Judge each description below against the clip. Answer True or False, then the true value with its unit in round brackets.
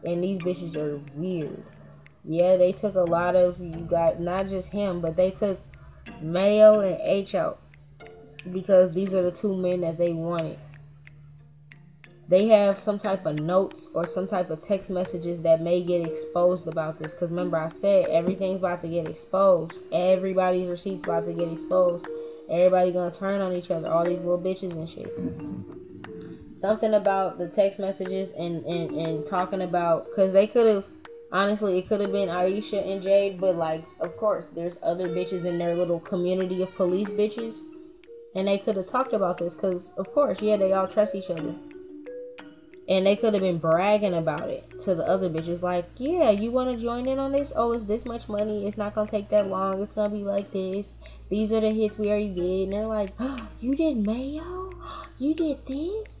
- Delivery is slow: False (195 wpm)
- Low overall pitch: False (185 Hz)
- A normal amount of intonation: True (3.5 semitones)